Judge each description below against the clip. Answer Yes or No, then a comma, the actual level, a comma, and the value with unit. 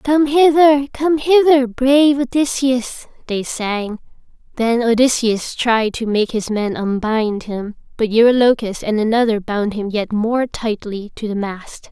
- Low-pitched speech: No, high, 235 Hz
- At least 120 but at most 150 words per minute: Yes, average, 145 wpm